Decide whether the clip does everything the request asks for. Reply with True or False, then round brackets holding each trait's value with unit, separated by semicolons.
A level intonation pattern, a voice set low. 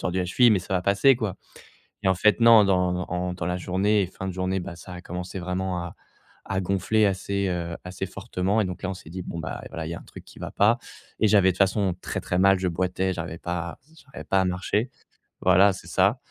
True (1.6 semitones; 95 Hz)